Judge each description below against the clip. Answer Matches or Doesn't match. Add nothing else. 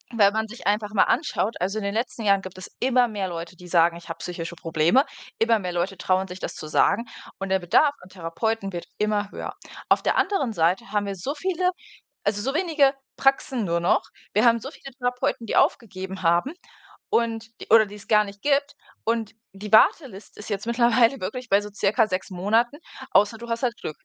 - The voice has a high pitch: Matches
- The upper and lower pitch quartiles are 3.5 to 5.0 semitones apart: Matches